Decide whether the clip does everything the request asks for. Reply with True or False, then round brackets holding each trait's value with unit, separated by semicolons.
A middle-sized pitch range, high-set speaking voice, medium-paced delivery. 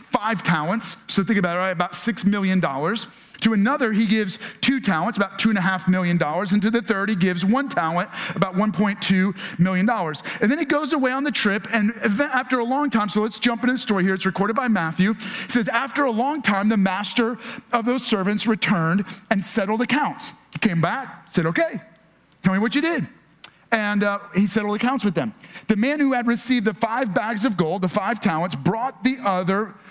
False (3.8 semitones; 210 Hz; 215 wpm)